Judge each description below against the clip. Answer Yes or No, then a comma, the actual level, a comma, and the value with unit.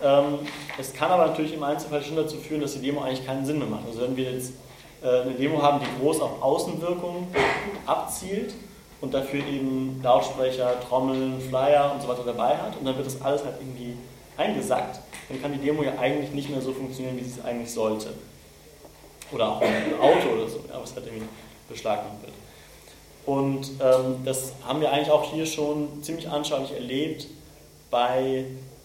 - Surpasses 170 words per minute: Yes, average, 180 wpm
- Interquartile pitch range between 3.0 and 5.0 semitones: No, narrow, 2.4 semitones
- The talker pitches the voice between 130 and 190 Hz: Yes, low, 135 Hz